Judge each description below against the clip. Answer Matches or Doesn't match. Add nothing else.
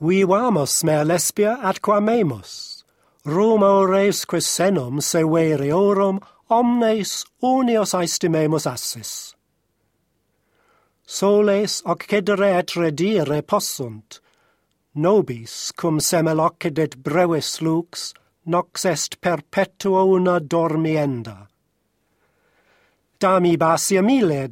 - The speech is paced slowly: Matches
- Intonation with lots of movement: Doesn't match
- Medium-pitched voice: Matches